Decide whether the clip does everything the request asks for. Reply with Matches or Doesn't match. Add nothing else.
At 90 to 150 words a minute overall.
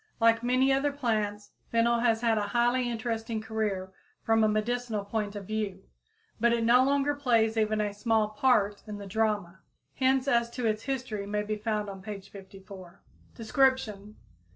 Doesn't match